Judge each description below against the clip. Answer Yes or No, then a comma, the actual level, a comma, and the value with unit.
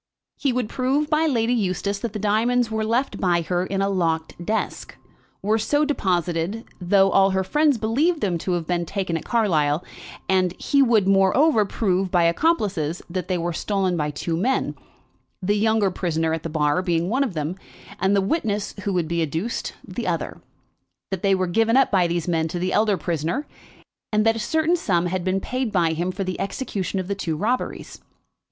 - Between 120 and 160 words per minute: No, average, 200 wpm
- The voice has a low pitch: No, high, 195 Hz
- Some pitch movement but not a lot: Yes, average, 4.4 semitones